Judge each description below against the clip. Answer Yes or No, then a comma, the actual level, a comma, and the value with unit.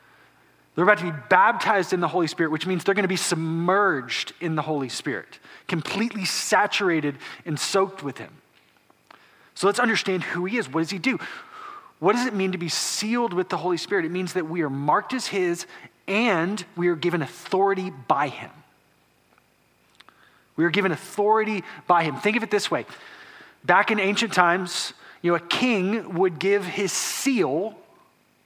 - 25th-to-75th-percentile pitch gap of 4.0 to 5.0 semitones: No, average, 3.4 semitones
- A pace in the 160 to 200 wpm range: Yes, average, 175 wpm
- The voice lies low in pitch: No, medium, 185 Hz